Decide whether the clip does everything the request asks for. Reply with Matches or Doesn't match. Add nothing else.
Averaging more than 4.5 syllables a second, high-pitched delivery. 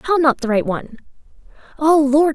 Matches